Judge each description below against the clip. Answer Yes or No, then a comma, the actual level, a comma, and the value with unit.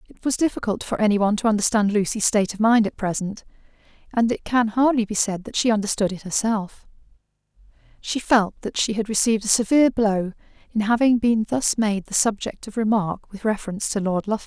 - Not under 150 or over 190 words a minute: No, average, 200 wpm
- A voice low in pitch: No, high, 215 Hz